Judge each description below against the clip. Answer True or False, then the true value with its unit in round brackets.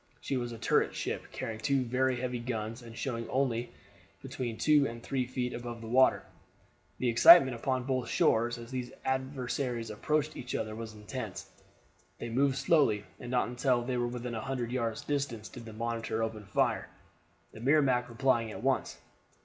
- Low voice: True (120 Hz)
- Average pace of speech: True (175 wpm)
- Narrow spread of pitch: True (2.2 semitones)